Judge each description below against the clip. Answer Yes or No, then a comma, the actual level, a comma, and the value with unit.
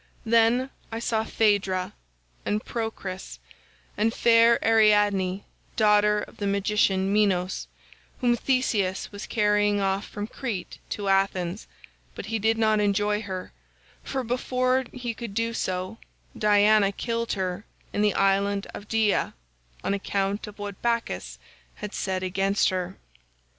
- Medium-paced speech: No, slow, 130 wpm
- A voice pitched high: Yes, high, 205 Hz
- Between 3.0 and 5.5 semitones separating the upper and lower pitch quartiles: No, narrow, 2.4 semitones